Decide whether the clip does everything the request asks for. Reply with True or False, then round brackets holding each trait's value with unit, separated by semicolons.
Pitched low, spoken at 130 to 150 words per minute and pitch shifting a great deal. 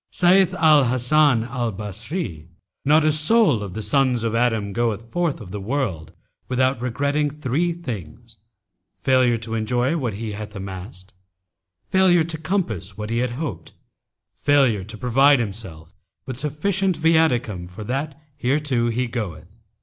True (125 Hz; 140 wpm; 5.8 semitones)